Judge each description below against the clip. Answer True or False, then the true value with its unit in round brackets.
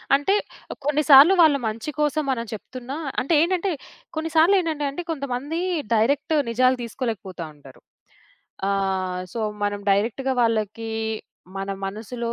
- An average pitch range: False (6.0 semitones)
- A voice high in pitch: True (255 Hz)